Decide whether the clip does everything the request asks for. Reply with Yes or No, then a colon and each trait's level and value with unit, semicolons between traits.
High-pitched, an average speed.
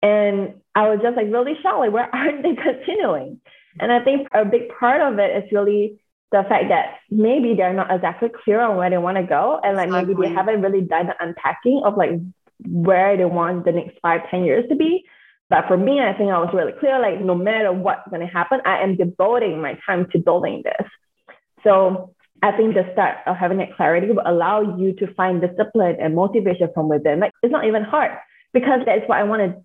No: high, 200 Hz; fast, 225 wpm